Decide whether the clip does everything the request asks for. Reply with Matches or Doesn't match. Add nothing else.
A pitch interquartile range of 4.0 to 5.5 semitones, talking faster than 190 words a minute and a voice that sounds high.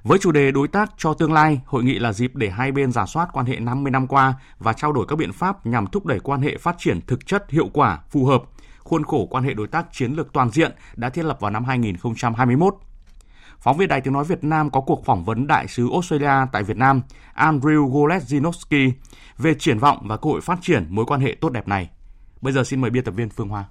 Doesn't match